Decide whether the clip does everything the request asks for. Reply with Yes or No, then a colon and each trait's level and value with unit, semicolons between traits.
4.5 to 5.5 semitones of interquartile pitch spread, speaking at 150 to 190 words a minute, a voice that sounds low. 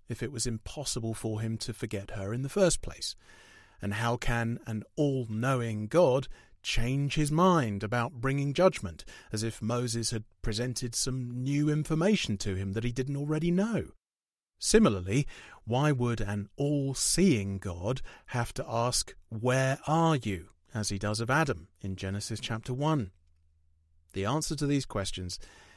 Yes: average, 5.0 semitones; average, 160 wpm; low, 120 Hz